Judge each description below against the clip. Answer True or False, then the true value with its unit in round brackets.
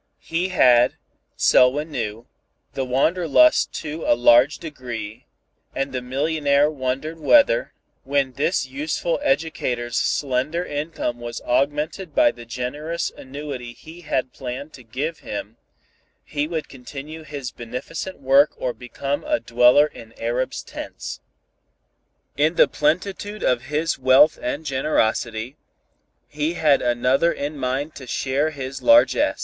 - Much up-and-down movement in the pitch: False (3.8 semitones)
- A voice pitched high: False (140 Hz)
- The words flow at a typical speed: False (130 wpm)